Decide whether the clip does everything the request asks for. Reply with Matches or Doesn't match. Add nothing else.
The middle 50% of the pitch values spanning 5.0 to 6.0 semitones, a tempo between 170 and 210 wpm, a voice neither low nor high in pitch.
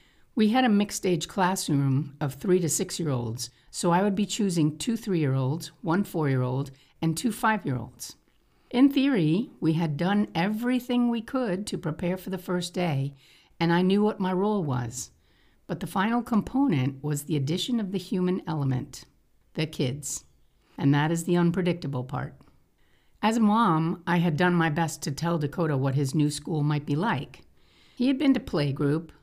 Matches